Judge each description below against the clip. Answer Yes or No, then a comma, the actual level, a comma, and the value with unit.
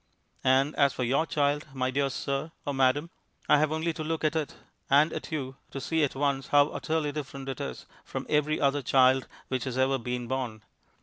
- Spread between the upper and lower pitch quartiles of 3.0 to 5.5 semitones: No, narrow, 2.4 semitones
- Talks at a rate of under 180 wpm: No, fast, 205 wpm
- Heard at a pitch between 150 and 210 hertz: No, medium, 140 Hz